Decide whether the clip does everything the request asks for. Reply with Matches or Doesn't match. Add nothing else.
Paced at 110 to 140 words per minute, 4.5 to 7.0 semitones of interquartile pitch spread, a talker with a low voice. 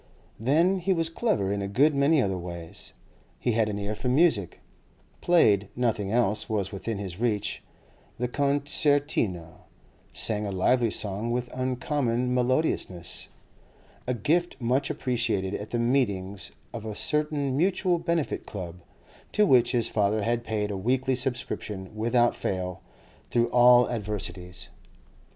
Matches